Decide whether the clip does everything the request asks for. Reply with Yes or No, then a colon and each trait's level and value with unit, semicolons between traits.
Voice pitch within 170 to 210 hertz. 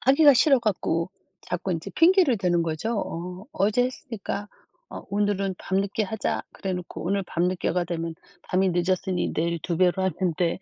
Yes: high, 190 Hz